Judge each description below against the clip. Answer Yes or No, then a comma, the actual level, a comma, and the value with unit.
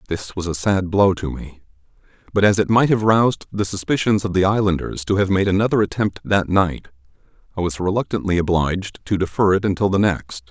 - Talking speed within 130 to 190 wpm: No, average, 200 wpm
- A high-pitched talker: No, very low, 95 Hz